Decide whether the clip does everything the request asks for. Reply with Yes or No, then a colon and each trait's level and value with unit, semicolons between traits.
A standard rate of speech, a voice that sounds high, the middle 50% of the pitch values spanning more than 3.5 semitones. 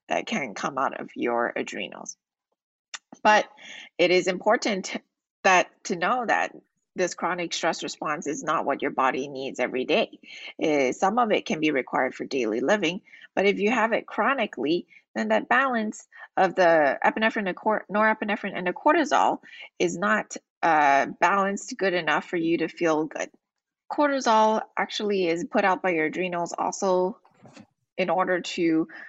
Yes: average, 160 wpm; high, 195 Hz; average, 4.3 semitones